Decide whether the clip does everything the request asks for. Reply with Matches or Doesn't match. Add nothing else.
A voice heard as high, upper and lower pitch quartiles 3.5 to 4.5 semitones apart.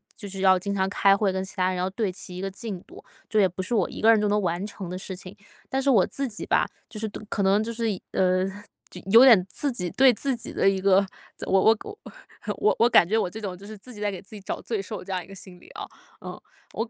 Doesn't match